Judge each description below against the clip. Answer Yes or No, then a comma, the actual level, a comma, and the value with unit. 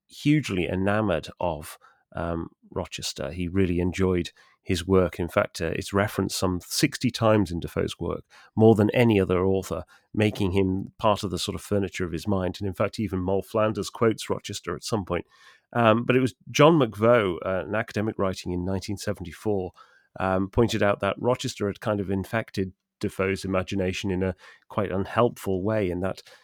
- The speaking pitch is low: Yes, low, 100 Hz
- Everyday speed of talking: Yes, average, 175 wpm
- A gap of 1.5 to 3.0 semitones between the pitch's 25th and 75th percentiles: Yes, narrow, 2.6 semitones